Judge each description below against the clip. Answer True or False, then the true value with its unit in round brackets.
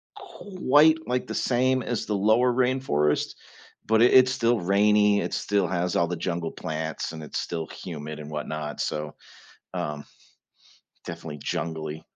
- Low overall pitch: True (95 Hz)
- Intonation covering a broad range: True (7.9 semitones)